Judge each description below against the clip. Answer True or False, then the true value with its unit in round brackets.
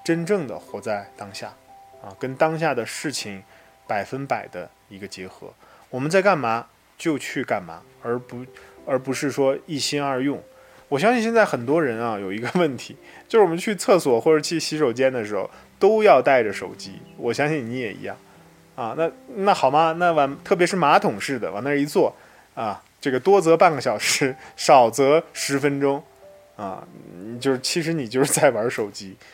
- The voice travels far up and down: False (4.5 semitones)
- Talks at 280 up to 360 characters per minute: False (260 characters per minute)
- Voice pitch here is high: False (140 Hz)